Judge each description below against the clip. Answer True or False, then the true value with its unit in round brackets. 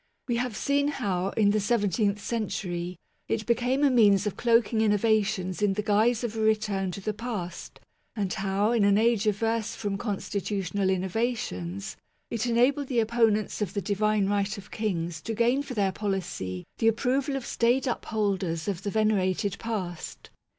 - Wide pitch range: False (3.0 semitones)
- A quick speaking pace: False (170 wpm)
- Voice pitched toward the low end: False (210 Hz)